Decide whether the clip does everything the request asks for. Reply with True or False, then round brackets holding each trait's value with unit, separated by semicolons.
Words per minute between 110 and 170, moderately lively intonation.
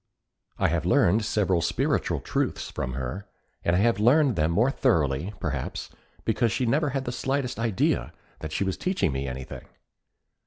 False (165 wpm; 8.0 semitones)